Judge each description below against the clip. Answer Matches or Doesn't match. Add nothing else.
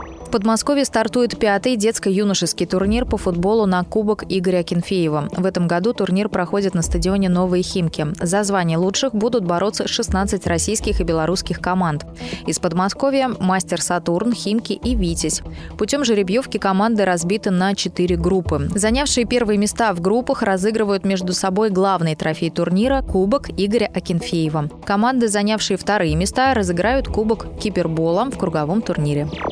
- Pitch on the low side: Doesn't match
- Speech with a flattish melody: Doesn't match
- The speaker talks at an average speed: Matches